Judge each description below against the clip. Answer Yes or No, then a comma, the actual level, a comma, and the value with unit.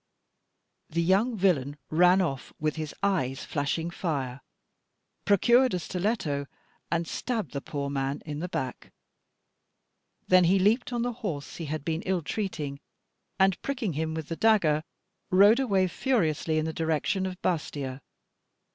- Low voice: No, medium, 170 Hz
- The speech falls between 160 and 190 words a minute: No, average, 145 wpm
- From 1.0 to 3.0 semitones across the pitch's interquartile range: No, average, 4.8 semitones